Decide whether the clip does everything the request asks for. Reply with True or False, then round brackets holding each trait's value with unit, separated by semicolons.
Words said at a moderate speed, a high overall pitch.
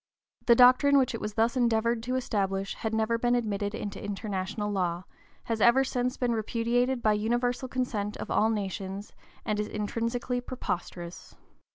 True (160 wpm; 225 Hz)